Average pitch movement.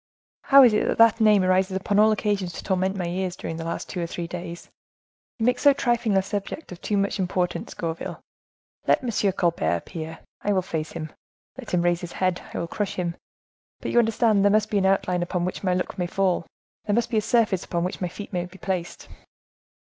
Yes: average, 3.2 semitones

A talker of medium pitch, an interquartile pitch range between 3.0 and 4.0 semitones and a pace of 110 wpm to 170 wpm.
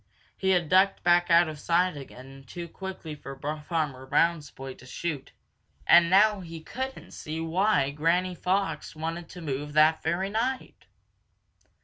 Yes: medium, 170 Hz; average, 3.6 semitones; average, 155 wpm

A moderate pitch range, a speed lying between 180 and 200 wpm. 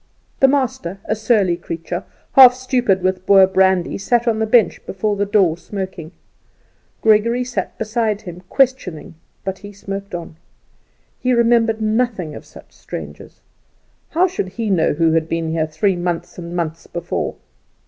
No: average, 5.0 semitones; average, 150 wpm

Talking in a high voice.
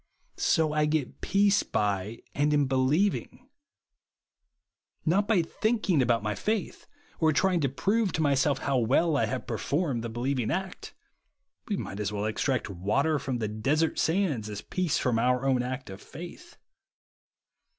No: medium, 140 Hz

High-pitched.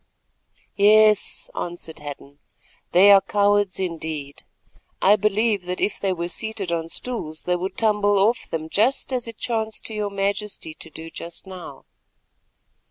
Yes: high, 195 Hz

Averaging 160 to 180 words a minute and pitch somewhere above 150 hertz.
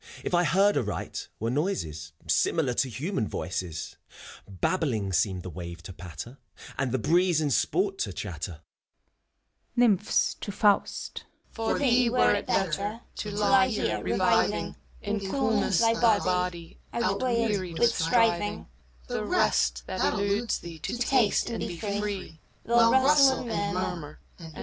No: average, 140 wpm; high, 190 Hz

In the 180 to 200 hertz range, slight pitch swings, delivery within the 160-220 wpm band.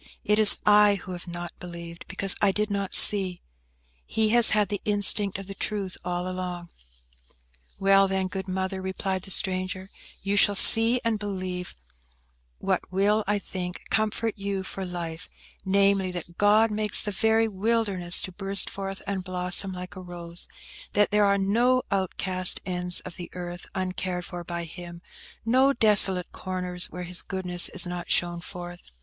Yes: high, 190 Hz; narrow, 2.3 semitones; average, 165 wpm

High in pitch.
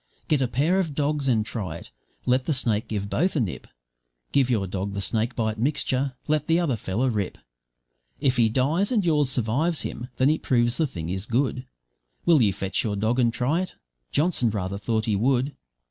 No: low, 125 Hz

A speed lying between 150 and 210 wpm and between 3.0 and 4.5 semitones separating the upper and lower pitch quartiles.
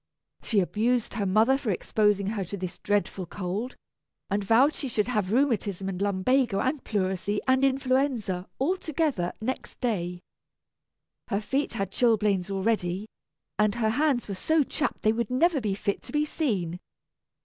No: average, 160 wpm; average, 5.0 semitones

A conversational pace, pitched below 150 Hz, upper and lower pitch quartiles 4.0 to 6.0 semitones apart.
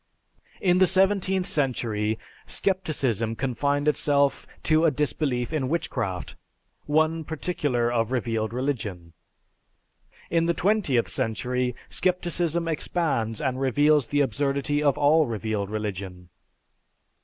No: slow, 110 wpm; medium, 140 Hz; wide, 5.6 semitones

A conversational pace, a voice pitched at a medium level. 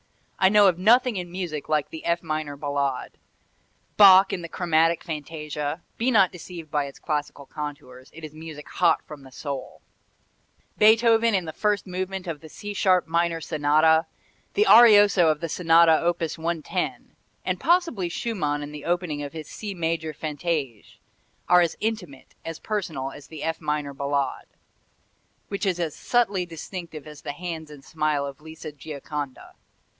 Yes: average, 165 wpm; medium, 160 Hz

